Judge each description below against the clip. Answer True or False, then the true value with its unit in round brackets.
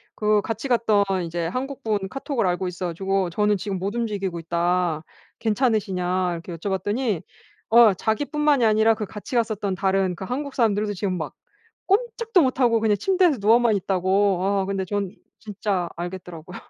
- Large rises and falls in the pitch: False (3.9 semitones)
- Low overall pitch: False (205 Hz)